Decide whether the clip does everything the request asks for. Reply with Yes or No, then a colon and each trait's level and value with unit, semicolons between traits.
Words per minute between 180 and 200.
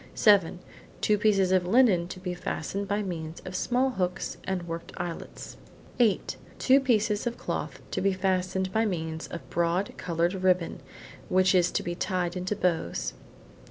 No: average, 160 wpm